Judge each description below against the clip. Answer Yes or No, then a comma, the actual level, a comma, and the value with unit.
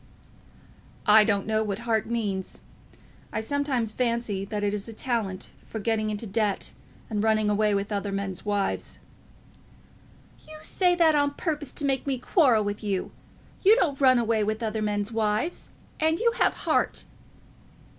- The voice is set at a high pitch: Yes, high, 220 Hz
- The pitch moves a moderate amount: Yes, average, 4.1 semitones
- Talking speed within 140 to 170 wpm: Yes, average, 160 wpm